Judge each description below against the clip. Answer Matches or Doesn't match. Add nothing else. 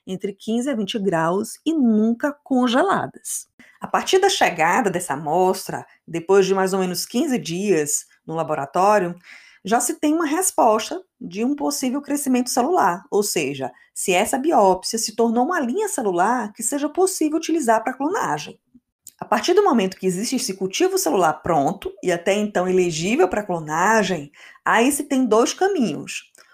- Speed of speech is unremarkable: Matches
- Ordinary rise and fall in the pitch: Doesn't match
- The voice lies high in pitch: Matches